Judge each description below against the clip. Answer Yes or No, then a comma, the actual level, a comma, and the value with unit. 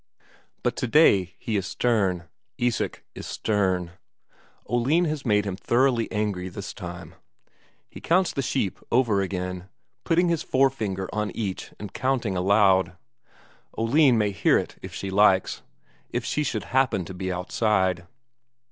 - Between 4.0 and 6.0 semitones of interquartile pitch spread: Yes, average, 4.7 semitones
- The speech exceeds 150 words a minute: No, average, 140 wpm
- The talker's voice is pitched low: Yes, low, 105 Hz